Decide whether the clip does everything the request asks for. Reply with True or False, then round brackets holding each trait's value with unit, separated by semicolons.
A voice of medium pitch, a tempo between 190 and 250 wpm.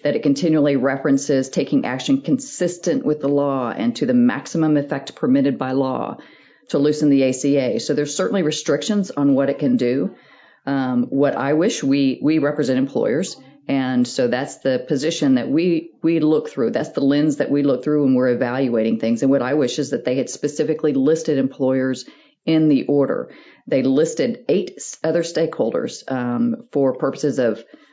False (145 Hz; 180 wpm)